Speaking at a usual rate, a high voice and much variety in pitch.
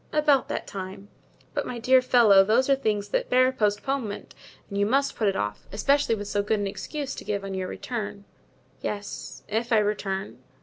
No: average, 190 wpm; high, 210 Hz; average, 4.2 semitones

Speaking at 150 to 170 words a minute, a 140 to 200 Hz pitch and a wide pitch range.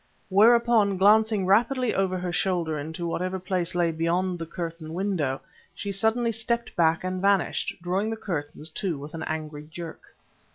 No: average, 160 wpm; medium, 185 Hz; average, 3.6 semitones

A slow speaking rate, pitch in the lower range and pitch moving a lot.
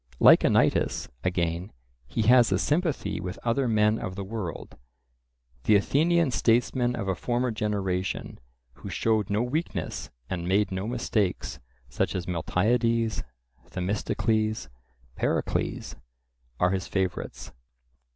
No: slow, 120 wpm; low, 105 Hz; average, 4.3 semitones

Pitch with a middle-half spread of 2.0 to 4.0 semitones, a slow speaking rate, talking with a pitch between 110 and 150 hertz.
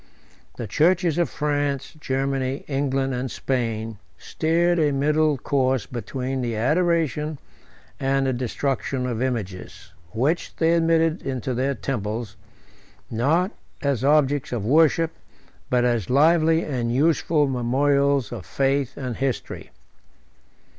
Yes: average, 3.6 semitones; slow, 120 wpm; low, 135 Hz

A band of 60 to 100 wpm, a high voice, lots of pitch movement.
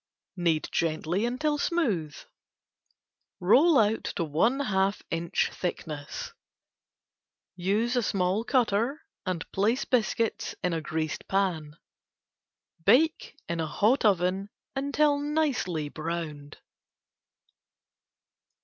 Yes: slow, 90 wpm; high, 195 Hz; wide, 7.0 semitones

